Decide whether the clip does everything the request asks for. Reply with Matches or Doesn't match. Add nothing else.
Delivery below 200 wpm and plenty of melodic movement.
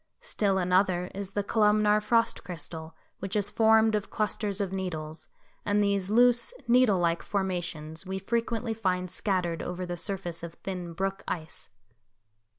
Doesn't match